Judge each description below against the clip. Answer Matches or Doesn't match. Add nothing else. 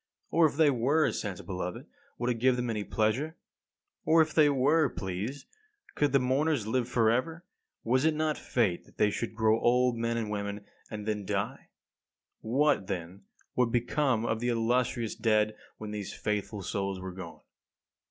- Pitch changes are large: Doesn't match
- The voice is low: Matches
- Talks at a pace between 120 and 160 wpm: Doesn't match